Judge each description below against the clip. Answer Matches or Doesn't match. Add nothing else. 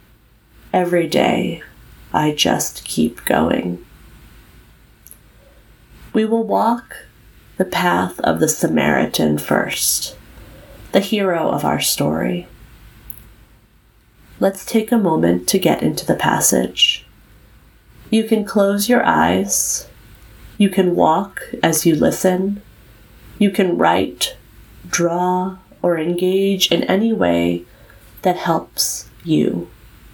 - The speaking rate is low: Matches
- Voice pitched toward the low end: Doesn't match